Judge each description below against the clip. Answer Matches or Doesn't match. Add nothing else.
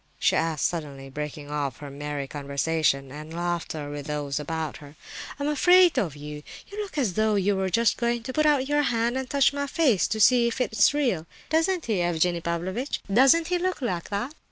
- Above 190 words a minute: Matches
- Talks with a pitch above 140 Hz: Matches